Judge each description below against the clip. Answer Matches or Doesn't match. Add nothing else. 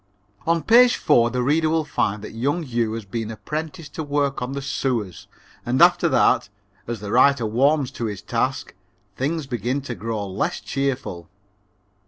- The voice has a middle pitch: Doesn't match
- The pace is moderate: Matches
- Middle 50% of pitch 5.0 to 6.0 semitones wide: Doesn't match